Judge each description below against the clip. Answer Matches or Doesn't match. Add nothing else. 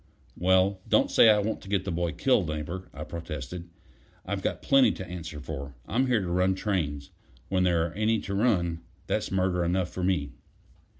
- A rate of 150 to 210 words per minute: Matches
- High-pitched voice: Doesn't match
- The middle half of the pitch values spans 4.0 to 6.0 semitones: Doesn't match